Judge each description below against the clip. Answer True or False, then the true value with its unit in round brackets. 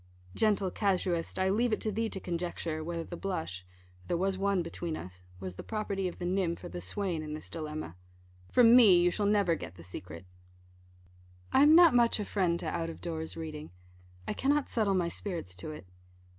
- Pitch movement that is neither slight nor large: True (4.4 semitones)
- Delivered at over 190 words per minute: True (205 wpm)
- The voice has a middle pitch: True (175 Hz)